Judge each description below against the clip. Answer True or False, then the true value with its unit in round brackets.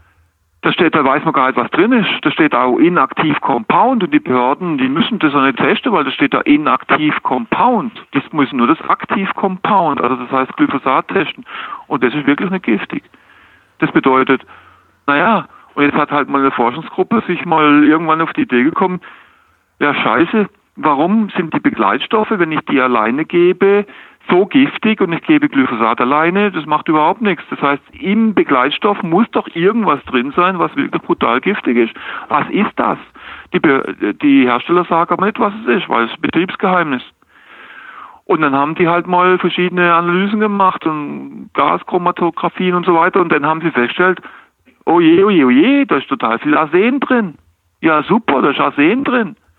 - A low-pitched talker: False (175 Hz)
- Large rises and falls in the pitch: True (6.6 semitones)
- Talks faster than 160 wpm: True (185 wpm)